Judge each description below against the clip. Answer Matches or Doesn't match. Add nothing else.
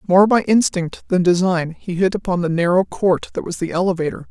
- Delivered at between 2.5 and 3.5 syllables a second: Doesn't match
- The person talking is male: Doesn't match